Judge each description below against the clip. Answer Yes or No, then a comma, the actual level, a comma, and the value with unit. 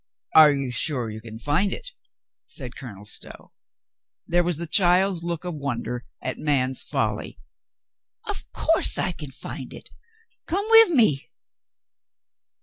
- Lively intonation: Yes, wide, 5.7 semitones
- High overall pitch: No, medium, 150 Hz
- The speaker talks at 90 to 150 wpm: Yes, average, 140 wpm